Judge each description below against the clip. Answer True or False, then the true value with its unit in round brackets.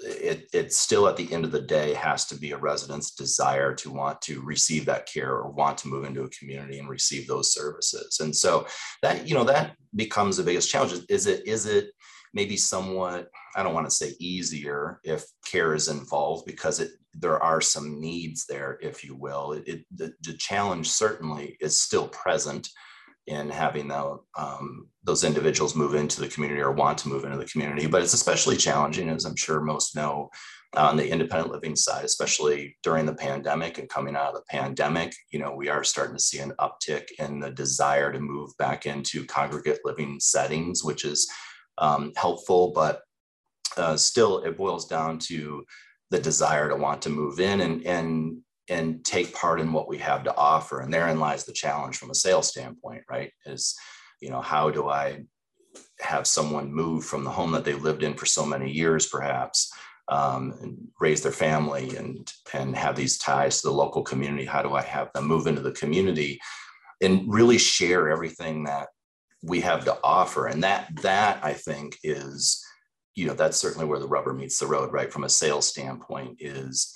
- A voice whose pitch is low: True (75 Hz)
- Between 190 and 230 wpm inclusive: True (195 wpm)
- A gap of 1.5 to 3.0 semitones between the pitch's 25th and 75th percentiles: True (2.6 semitones)